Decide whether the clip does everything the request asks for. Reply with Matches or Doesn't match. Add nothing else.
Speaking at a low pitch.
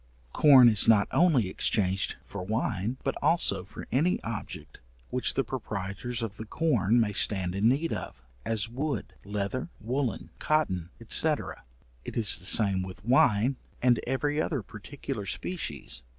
Matches